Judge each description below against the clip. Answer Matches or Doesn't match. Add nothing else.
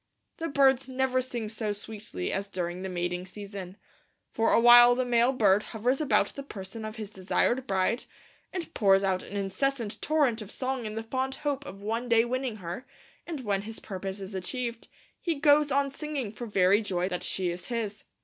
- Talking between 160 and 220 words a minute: Matches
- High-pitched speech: Matches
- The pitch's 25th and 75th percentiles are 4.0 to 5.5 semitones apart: Matches